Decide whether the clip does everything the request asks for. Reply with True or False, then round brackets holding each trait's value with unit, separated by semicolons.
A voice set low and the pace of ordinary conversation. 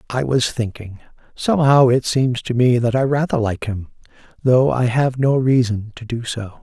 True (125 Hz; 190 wpm)